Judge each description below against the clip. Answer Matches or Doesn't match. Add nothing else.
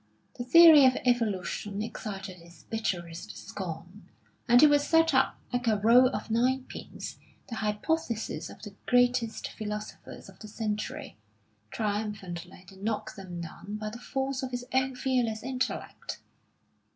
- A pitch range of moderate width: Matches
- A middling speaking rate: Matches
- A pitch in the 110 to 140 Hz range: Doesn't match